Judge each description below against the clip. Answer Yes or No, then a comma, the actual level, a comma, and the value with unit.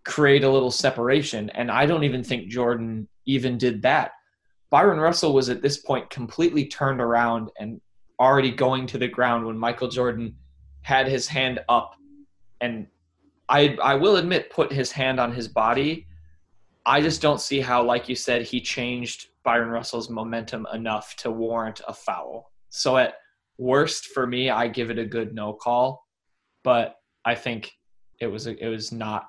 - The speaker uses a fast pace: No, average, 175 wpm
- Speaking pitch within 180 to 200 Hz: No, low, 125 Hz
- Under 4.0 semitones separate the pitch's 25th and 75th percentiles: Yes, average, 2.8 semitones